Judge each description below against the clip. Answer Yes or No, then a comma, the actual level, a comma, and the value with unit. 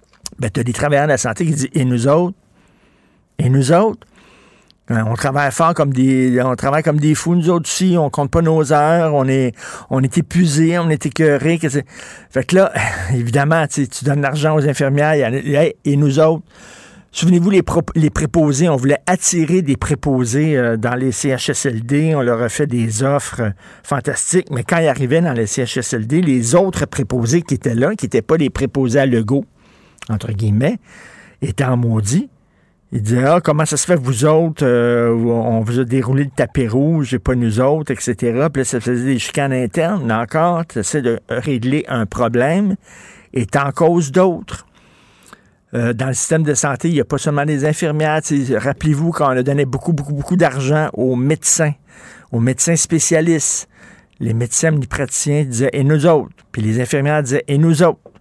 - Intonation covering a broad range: No, average, 3.9 semitones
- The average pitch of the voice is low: No, medium, 145 Hz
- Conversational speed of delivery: Yes, average, 190 wpm